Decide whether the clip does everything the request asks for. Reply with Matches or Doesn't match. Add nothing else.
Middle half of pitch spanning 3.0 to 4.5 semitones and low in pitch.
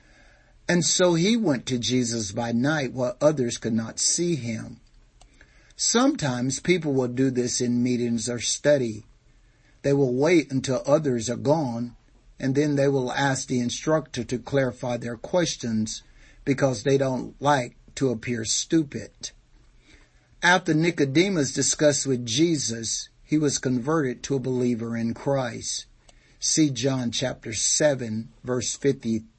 Matches